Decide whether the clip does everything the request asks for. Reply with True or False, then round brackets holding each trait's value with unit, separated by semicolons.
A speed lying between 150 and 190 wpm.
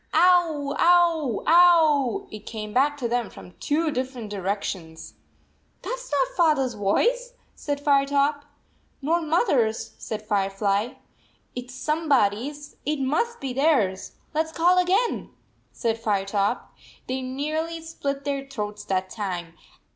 False (140 wpm)